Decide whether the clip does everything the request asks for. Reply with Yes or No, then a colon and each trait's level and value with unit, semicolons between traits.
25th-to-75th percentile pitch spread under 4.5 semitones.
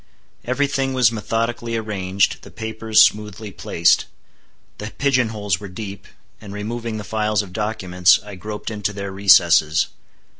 Yes: narrow, 2.5 semitones